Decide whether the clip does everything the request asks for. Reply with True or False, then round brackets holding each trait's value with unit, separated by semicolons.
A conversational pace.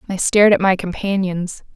True (170 wpm)